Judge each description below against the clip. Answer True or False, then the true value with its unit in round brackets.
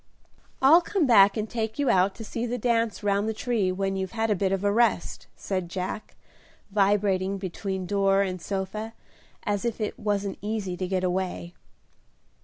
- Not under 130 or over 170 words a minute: False (180 wpm)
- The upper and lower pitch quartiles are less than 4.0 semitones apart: True (2.7 semitones)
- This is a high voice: True (200 Hz)